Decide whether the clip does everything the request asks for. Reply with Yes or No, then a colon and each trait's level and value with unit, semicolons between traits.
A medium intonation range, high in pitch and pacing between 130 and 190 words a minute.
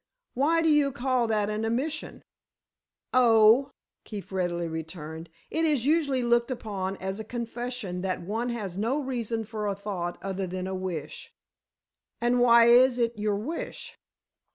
Yes: average, 4.6 semitones; high, 225 Hz; average, 155 wpm